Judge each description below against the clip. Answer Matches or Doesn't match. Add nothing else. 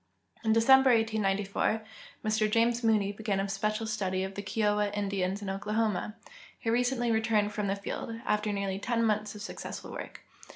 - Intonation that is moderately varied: Doesn't match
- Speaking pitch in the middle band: Doesn't match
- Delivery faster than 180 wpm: Doesn't match